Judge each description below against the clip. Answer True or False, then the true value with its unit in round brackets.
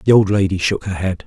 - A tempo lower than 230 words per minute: False (285 wpm)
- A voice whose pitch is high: False (100 Hz)